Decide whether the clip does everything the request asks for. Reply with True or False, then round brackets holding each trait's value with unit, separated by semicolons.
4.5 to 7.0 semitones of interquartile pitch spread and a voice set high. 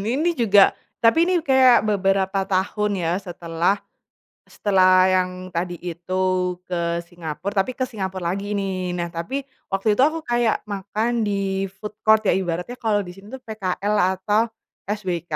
False (3.0 semitones; 195 Hz)